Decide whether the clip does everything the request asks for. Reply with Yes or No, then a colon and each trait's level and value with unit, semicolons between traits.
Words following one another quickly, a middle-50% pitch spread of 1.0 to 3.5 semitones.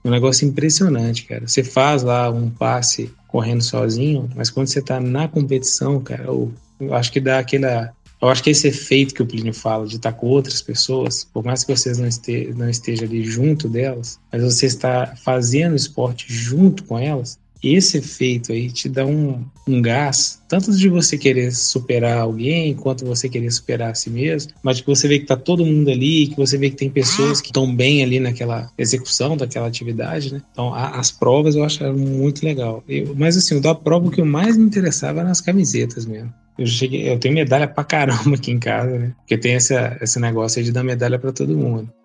Yes: fast, 210 wpm; average, 3.1 semitones